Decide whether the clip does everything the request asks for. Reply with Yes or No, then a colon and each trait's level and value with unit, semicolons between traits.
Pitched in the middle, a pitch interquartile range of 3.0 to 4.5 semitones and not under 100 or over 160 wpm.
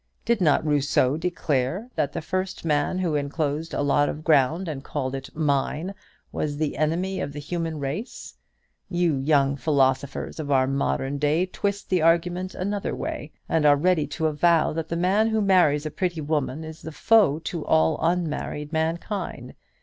No: medium, 155 Hz; average, 3.6 semitones; average, 175 wpm